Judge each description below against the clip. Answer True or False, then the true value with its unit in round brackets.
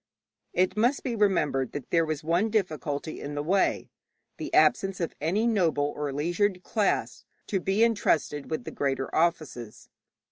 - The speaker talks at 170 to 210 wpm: False (155 wpm)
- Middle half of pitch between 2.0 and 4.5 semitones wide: False (5.3 semitones)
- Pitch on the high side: False (170 Hz)